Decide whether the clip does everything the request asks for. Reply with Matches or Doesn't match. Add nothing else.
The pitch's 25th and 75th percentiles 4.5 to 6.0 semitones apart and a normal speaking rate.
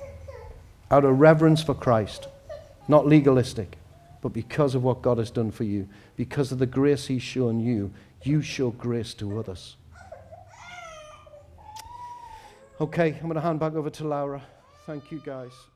Matches